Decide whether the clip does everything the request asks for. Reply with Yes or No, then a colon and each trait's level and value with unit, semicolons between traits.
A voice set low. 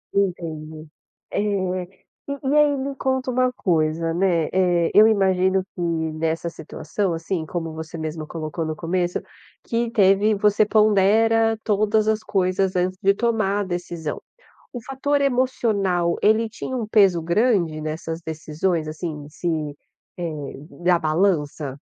No: medium, 185 Hz